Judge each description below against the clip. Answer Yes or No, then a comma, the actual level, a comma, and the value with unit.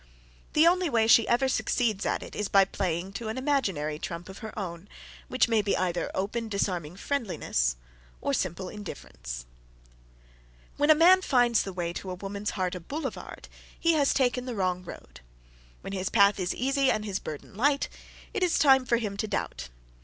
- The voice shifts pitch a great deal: Yes, wide, 5.8 semitones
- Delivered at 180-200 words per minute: Yes, average, 185 wpm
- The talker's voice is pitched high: Yes, high, 205 Hz